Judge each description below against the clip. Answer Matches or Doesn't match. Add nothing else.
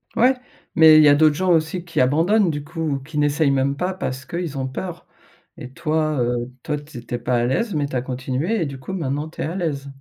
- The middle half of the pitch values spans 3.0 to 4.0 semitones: Matches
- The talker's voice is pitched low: Doesn't match